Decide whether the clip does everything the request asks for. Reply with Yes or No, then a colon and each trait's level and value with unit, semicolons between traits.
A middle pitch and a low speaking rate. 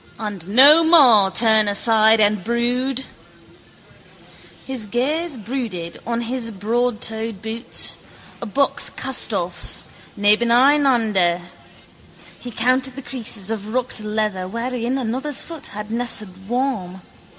No: high, 230 Hz; slow, 105 wpm